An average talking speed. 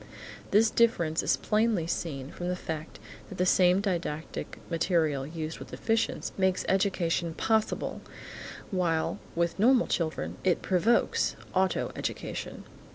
No: slow, 125 wpm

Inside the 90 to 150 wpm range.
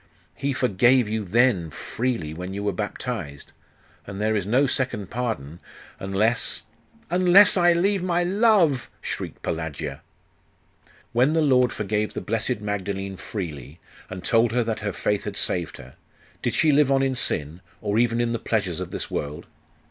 No: average, 165 wpm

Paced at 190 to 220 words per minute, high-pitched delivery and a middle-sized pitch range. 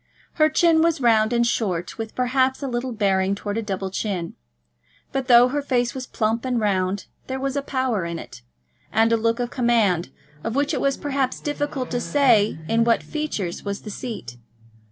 Yes: average, 195 wpm; high, 235 Hz; average, 4.3 semitones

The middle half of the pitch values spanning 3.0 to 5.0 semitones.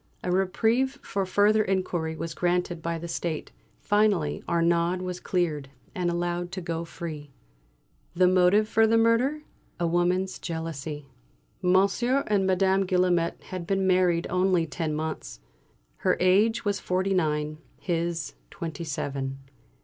No: narrow, 2.5 semitones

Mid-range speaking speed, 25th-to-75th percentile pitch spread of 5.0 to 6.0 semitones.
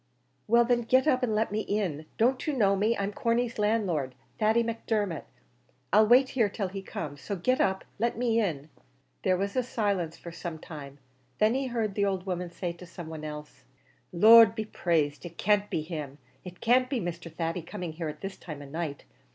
No: fast, 210 wpm; average, 5.3 semitones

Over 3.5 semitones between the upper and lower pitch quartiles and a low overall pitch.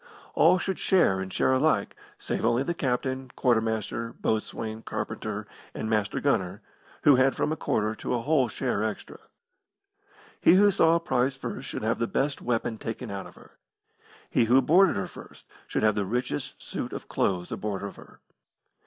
Yes: average, 4.2 semitones; low, 120 Hz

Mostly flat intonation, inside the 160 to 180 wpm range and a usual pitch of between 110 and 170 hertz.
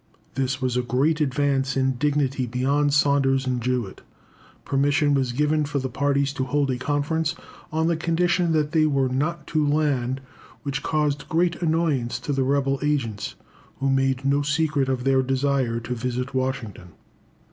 Yes: narrow, 2.3 semitones; average, 165 wpm; medium, 140 Hz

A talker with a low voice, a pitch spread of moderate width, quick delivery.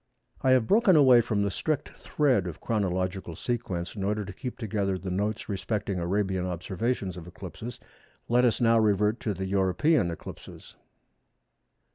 No: low, 105 Hz; average, 4.2 semitones; average, 155 wpm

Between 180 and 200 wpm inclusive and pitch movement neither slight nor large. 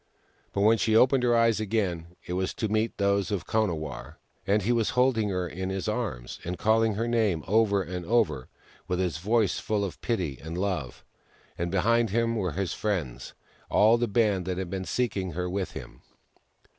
Yes: average, 195 wpm; average, 3.9 semitones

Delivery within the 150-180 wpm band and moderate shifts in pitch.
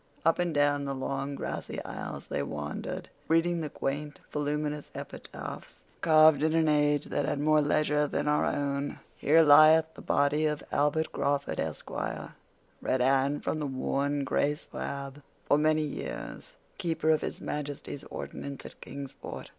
No: average, 155 wpm; narrow, 1.7 semitones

